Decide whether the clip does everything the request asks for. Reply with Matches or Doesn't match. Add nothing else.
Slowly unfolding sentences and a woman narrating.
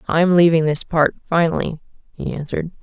Matches